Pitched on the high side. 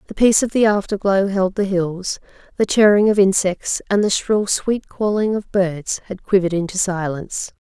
Yes: high, 195 Hz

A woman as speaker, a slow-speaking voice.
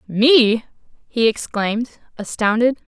Yes: female; slow, 80 wpm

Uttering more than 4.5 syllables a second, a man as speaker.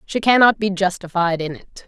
No: 5.2 syllables/s; female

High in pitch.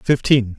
No: low, 120 Hz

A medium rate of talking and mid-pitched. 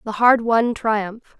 No: average, 170 wpm; high, 225 Hz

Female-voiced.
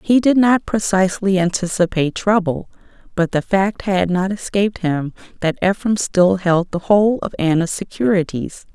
Yes: female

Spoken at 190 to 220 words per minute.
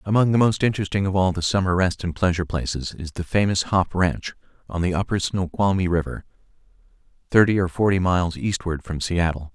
No: average, 180 wpm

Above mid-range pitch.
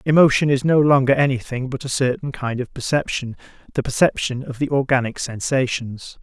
No: low, 130 Hz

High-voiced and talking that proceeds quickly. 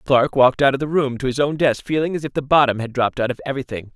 No: low, 135 Hz; fast, 305 wpm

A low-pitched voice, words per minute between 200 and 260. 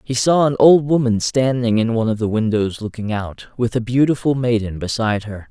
Yes: low, 115 Hz; fast, 205 wpm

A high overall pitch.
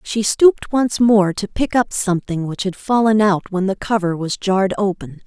Yes: high, 200 Hz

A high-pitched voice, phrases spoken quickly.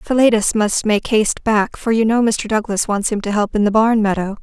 Yes: high, 215 Hz; fast, 245 wpm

